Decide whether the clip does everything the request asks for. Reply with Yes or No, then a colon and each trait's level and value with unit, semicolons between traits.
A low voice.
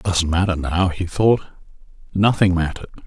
Yes: very low, 90 Hz